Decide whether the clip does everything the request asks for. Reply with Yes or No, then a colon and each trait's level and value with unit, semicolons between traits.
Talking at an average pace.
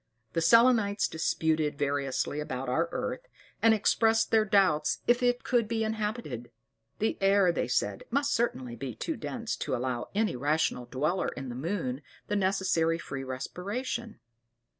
Yes: average, 150 wpm